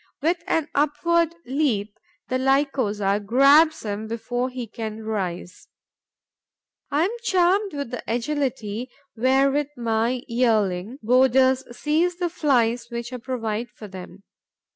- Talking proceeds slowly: Yes, slow, 120 wpm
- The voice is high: Yes, very high, 250 Hz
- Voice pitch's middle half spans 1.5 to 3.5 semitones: No, average, 4.7 semitones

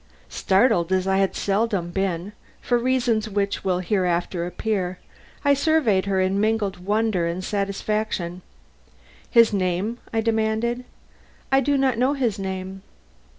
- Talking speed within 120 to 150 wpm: Yes, slow, 135 wpm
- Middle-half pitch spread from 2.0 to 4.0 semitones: Yes, average, 3.4 semitones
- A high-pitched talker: Yes, high, 200 Hz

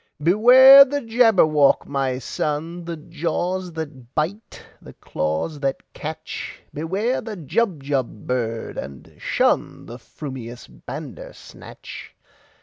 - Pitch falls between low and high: Yes, medium, 155 Hz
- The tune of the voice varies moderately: No, wide, 6.9 semitones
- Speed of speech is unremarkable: No, slow, 90 wpm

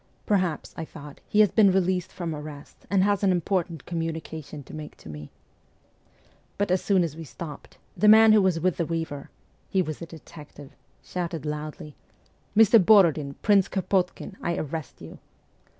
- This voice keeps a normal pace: Yes, average, 165 wpm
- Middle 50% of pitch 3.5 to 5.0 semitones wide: Yes, average, 3.8 semitones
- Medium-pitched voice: Yes, medium, 170 Hz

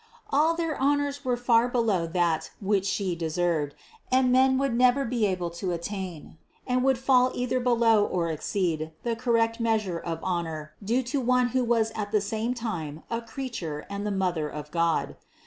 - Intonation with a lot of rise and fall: Yes, wide, 6.4 semitones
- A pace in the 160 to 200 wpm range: Yes, average, 180 wpm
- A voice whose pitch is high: Yes, high, 220 Hz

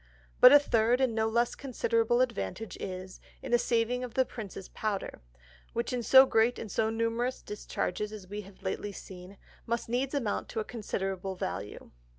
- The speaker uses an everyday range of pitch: Yes, average, 3.5 semitones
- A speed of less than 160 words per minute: No, average, 170 wpm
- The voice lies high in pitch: Yes, high, 225 Hz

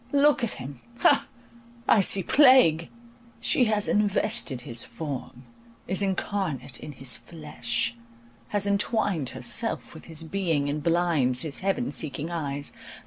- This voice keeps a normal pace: No, slow, 130 wpm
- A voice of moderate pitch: Yes, medium, 165 Hz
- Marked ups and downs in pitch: Yes, wide, 6.3 semitones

